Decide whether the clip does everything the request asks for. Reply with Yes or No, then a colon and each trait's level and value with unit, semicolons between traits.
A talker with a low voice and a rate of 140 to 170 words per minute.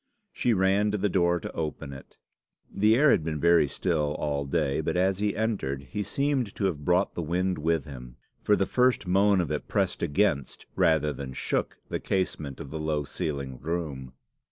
No: very low, 85 Hz; average, 195 wpm